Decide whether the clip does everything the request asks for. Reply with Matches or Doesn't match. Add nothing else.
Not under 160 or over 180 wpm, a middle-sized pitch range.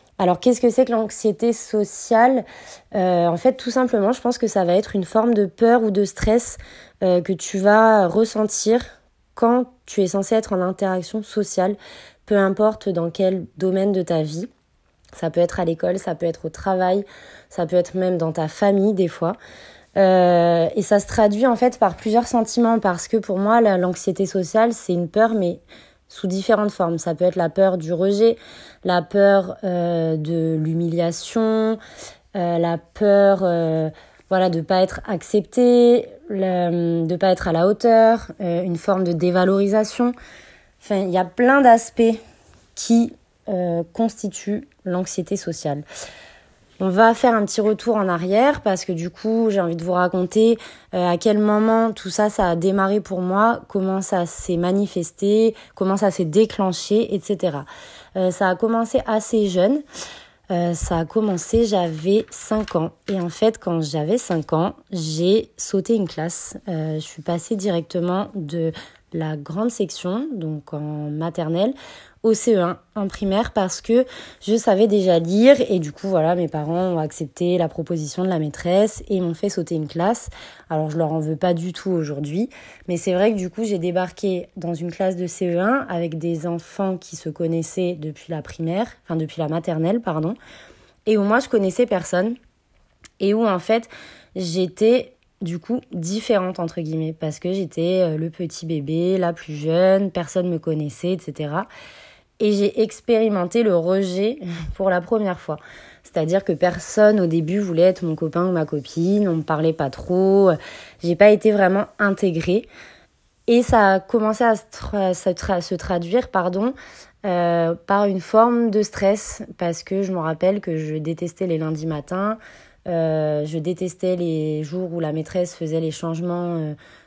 Matches